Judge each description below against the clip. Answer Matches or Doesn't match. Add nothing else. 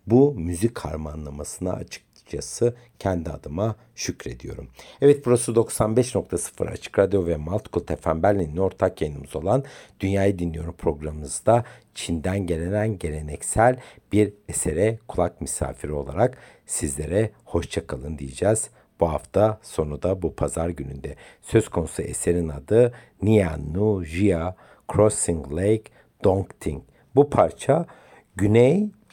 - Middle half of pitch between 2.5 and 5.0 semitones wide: Doesn't match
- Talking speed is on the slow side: Doesn't match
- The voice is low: Matches